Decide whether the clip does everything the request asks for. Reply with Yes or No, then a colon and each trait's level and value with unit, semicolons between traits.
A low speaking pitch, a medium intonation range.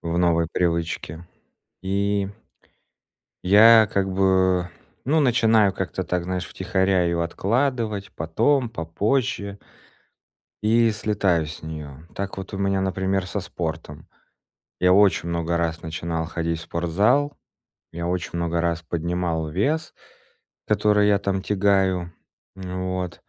Yes: very low, 95 Hz; average, 3.1 semitones